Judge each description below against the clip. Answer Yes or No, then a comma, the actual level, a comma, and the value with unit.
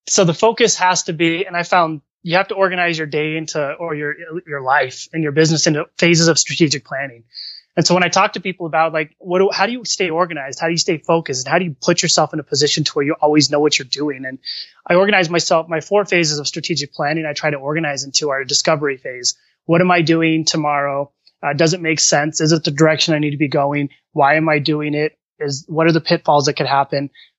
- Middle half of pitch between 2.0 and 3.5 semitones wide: Yes, average, 2.7 semitones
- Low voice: No, medium, 160 Hz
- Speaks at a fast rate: Yes, fast, 255 wpm